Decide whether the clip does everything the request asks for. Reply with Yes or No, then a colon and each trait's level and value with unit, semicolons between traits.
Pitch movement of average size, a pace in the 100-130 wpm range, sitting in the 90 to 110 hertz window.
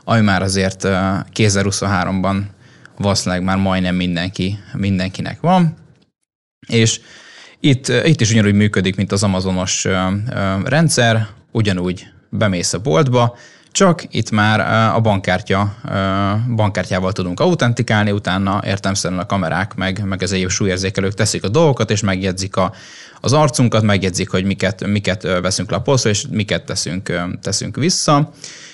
Yes: average, 3.5 semitones; average, 125 wpm; low, 100 Hz